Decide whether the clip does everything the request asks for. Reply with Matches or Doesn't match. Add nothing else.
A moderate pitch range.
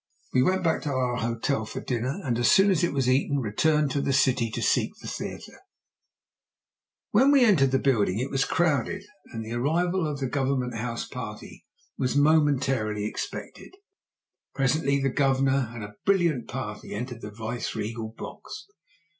Matches